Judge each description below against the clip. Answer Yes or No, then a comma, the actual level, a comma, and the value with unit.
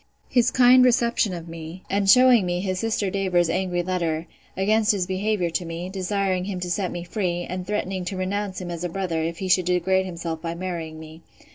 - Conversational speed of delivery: No, fast, 210 wpm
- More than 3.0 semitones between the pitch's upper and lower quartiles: No, narrow, 2.4 semitones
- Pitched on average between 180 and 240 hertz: Yes, medium, 185 Hz